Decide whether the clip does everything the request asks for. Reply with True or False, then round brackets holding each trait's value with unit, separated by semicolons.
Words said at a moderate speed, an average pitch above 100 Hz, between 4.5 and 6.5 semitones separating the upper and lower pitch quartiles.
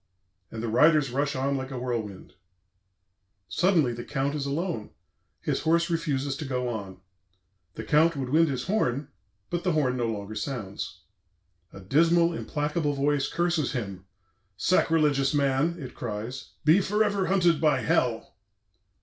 True (145 wpm; 140 Hz; 5.0 semitones)